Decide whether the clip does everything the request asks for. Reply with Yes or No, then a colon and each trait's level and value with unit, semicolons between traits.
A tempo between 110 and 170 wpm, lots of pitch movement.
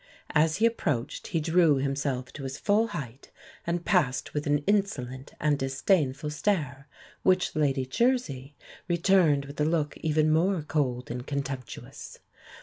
No: average, 145 wpm; average, 4.2 semitones